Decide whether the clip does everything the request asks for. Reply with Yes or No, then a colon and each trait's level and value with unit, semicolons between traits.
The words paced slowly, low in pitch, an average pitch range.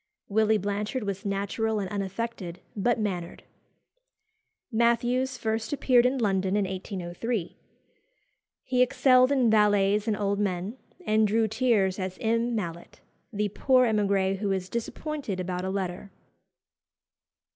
No: slow, 125 wpm; high, 210 Hz; average, 3.3 semitones